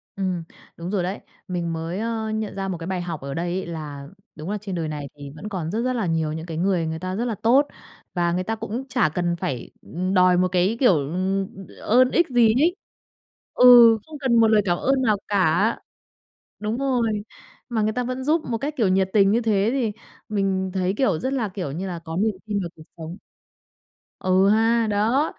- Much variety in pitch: No, average, 4.6 semitones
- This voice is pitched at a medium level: No, high, 195 Hz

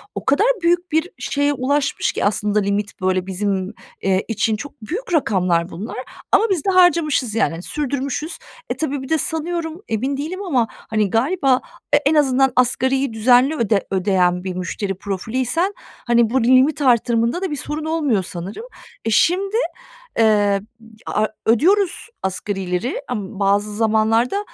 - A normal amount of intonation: No, wide, 6.8 semitones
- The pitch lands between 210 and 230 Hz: No, high, 245 Hz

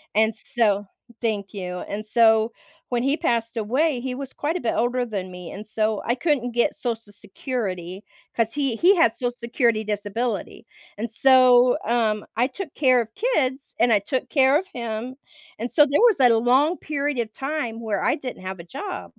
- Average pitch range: Yes, average, 3.7 semitones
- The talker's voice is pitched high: Yes, high, 240 Hz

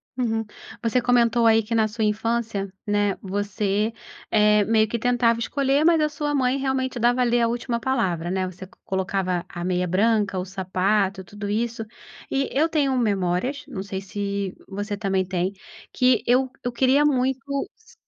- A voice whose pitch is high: Yes, high, 220 Hz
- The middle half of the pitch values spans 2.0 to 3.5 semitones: No, average, 4.3 semitones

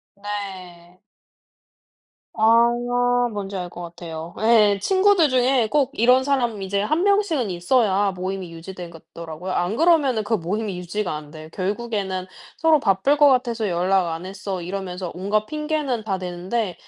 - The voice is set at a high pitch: Yes, high, 200 Hz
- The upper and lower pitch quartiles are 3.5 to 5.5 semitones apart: Yes, average, 5.2 semitones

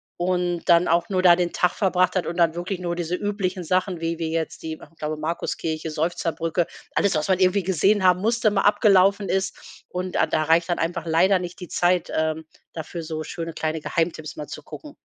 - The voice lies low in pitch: No, medium, 175 Hz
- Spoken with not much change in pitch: Yes, narrow, 2.2 semitones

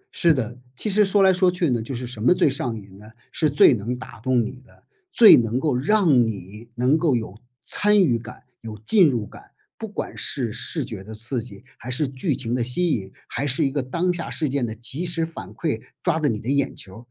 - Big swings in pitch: Yes, wide, 6.1 semitones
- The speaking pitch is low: Yes, low, 130 Hz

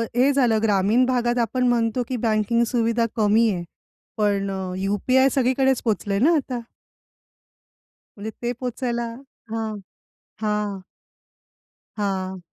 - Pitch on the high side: Yes, high, 230 Hz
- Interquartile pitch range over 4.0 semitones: No, average, 3.3 semitones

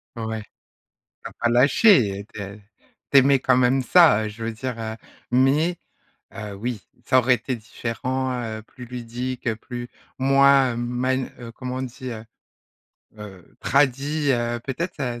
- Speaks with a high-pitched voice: No, low, 125 Hz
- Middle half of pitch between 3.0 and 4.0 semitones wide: No, narrow, 2.5 semitones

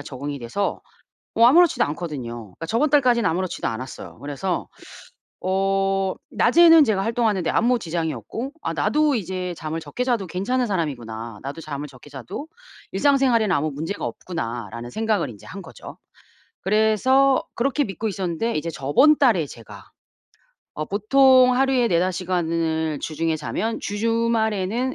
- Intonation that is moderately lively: No, wide, 7.2 semitones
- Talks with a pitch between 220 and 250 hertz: No, high, 190 Hz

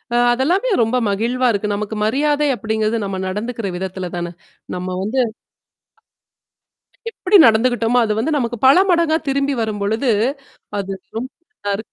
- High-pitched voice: Yes, high, 225 Hz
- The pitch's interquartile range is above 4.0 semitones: Yes, average, 4.7 semitones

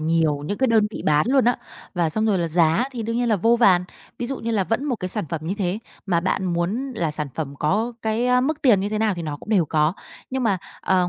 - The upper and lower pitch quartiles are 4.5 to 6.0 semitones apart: Yes, wide, 5.6 semitones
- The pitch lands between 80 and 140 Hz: No, high, 200 Hz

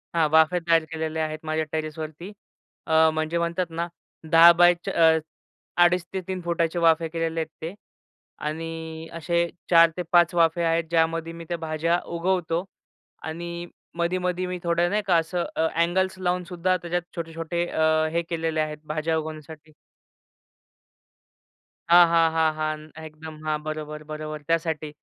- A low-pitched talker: No, medium, 165 Hz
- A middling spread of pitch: No, narrow, 1.4 semitones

